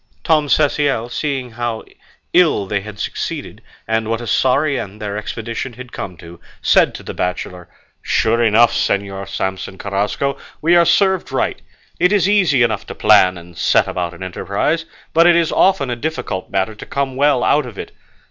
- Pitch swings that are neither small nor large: No, wide, 6.7 semitones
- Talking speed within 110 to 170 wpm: No, average, 180 wpm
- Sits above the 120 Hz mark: No, low, 115 Hz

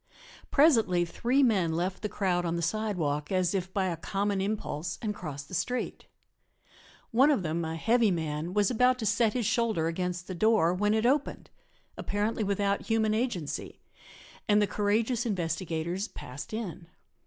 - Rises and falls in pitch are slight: No, average, 4.4 semitones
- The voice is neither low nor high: No, high, 200 Hz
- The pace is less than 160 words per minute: No, average, 165 wpm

